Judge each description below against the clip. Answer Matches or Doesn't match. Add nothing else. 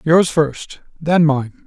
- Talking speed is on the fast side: Doesn't match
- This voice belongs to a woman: Doesn't match